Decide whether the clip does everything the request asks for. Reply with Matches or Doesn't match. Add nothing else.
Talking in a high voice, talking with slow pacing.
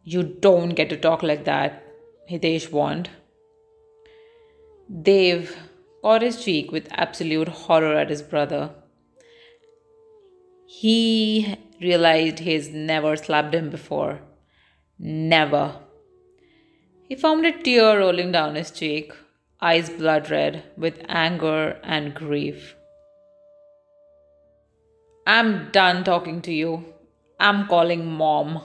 Doesn't match